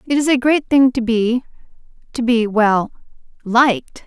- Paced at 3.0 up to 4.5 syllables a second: Yes, 4.4 syllables/s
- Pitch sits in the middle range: No, high, 240 Hz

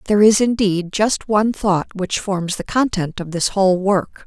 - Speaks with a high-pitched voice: Yes, high, 195 Hz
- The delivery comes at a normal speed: Yes, average, 195 wpm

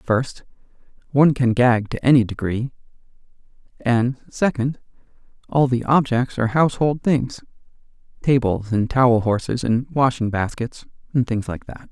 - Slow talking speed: Yes, slow, 125 wpm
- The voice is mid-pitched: No, low, 125 Hz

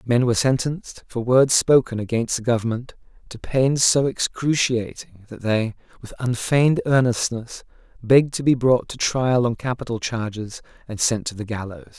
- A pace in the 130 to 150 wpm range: No, average, 160 wpm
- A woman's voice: No, male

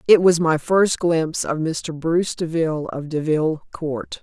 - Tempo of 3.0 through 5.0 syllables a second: Yes, 4.6 syllables/s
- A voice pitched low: No, medium, 160 Hz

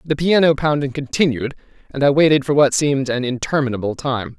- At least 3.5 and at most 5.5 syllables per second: No, 5.9 syllables/s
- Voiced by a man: Yes, male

